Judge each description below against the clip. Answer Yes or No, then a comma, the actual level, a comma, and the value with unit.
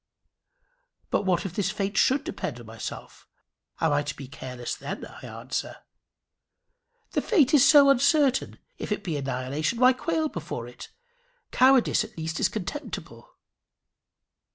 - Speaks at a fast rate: No, average, 145 wpm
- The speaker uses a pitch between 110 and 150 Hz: No, high, 195 Hz